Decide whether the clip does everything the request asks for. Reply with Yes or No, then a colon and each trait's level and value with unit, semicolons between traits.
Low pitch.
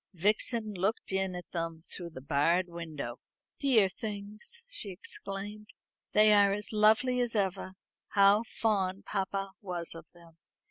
No: high, 195 Hz